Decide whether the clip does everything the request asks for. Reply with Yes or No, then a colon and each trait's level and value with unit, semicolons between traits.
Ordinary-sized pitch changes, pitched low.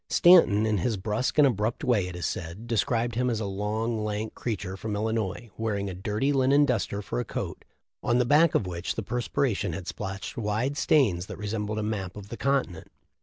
Yes: average, 3.3 semitones; low, 110 Hz